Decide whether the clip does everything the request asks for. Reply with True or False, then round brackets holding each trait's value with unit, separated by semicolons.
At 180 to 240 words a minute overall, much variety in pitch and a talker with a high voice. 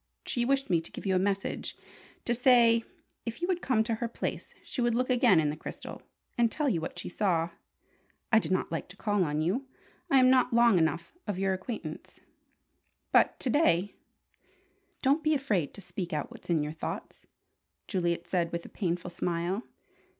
True (195 wpm; 6.0 semitones; 200 Hz)